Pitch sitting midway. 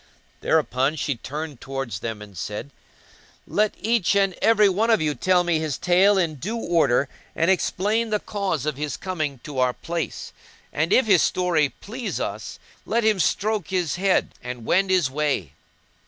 Yes: medium, 170 Hz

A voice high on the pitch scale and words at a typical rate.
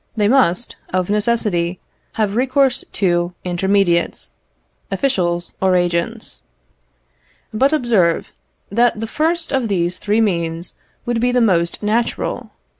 No: high, 205 Hz; slow, 115 wpm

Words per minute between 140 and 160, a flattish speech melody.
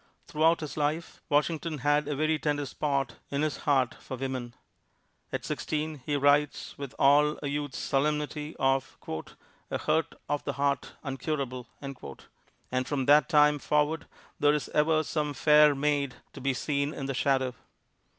Yes: average, 155 wpm; narrow, 1.7 semitones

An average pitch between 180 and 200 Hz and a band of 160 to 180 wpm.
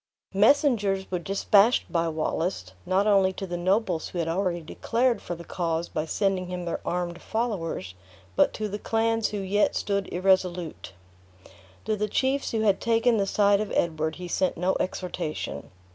Yes: high, 190 Hz; average, 170 wpm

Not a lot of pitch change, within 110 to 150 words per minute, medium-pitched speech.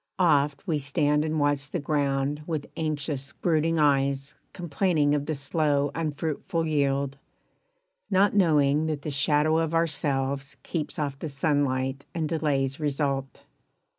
Yes: narrow, 2.2 semitones; slow, 135 wpm; medium, 145 Hz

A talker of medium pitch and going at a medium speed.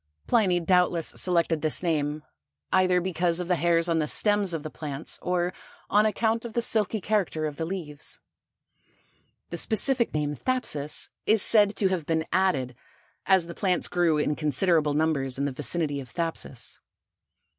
Yes: medium, 170 Hz; average, 165 wpm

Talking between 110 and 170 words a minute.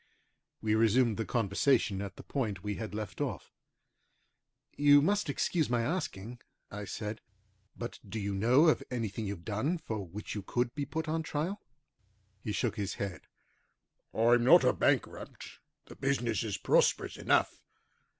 Yes: average, 155 wpm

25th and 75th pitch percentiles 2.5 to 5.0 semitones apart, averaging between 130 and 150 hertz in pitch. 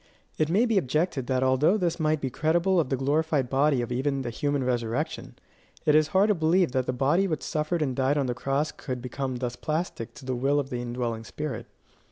Yes: average, 3.7 semitones; medium, 140 Hz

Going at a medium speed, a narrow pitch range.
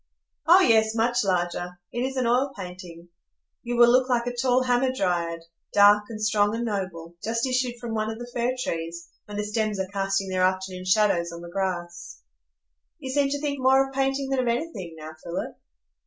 No: average, 195 wpm; wide, 5.4 semitones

